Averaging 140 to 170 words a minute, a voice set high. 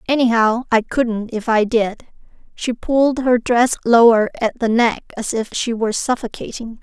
Yes: average, 165 wpm; high, 235 Hz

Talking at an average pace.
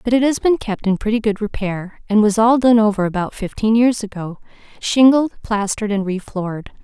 Yes: average, 195 wpm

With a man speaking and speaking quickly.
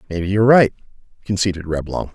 No: male; average, 140 wpm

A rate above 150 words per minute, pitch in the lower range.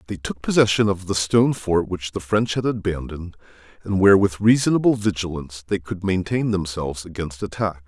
Yes: average, 175 wpm; very low, 95 Hz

